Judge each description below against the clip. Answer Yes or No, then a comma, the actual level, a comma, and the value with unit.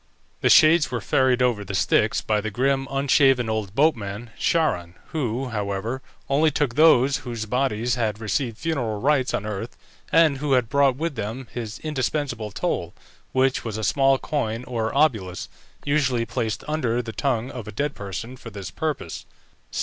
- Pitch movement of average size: Yes, average, 4.1 semitones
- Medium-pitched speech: No, low, 125 Hz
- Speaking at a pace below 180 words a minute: Yes, average, 165 wpm